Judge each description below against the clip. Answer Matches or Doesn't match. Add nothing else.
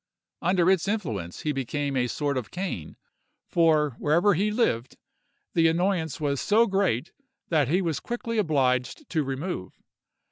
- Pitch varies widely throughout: Matches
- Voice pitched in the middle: Matches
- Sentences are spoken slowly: Doesn't match